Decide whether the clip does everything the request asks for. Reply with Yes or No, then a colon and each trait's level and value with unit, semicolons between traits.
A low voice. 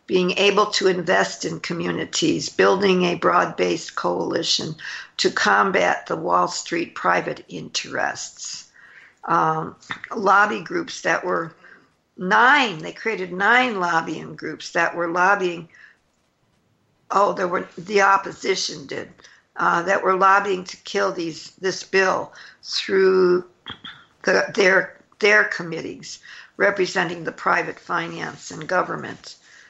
No: medium, 185 Hz